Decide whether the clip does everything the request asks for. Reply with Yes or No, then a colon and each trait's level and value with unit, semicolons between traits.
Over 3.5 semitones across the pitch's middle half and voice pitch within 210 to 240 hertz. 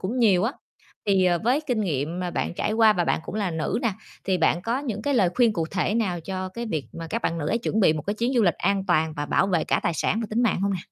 No: average, 4.7 semitones; high, 195 Hz